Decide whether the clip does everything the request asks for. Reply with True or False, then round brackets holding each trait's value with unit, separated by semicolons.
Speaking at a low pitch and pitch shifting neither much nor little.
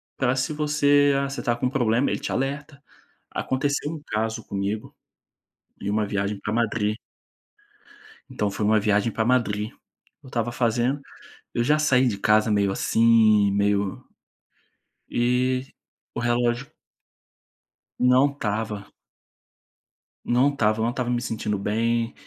True (115 Hz; 3.5 semitones)